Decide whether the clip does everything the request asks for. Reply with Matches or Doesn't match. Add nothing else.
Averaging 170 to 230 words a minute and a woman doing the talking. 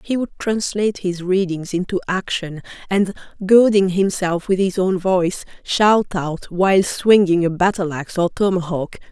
Doesn't match